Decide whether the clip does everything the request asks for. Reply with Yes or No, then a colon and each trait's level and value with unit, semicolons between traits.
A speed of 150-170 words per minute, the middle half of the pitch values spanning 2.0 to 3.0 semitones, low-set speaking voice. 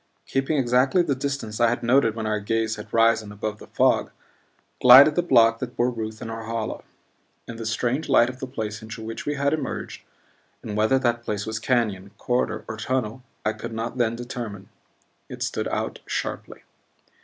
No: average, 185 wpm; narrow, 2.6 semitones; low, 115 Hz